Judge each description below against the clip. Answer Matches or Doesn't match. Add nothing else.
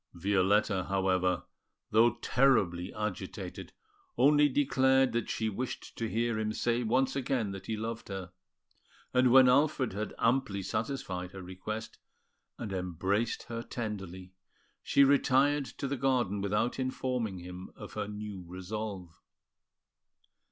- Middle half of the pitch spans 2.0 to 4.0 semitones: Doesn't match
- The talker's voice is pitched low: Matches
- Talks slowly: Matches